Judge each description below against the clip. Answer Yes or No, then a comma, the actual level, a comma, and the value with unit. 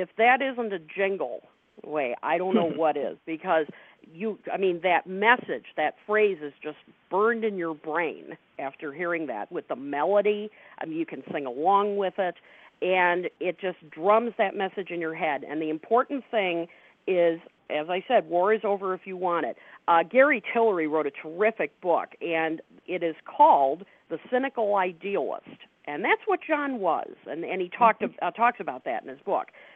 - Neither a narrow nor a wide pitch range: Yes, average, 4.8 semitones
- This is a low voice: No, high, 190 Hz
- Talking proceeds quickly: No, average, 190 wpm